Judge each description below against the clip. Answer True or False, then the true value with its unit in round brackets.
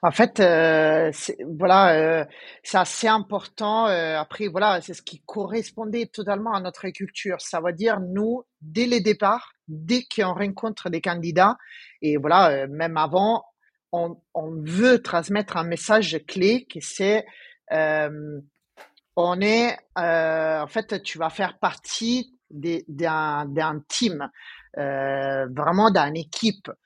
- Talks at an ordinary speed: False (140 wpm)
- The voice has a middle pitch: True (180 Hz)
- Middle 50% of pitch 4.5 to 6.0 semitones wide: True (5.4 semitones)